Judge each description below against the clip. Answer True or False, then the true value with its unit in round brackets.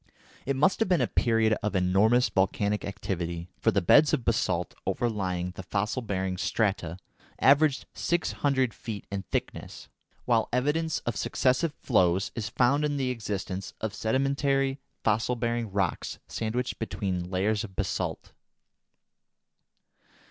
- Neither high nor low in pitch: False (110 Hz)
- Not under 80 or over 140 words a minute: True (135 wpm)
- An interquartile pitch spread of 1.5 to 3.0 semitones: False (5.2 semitones)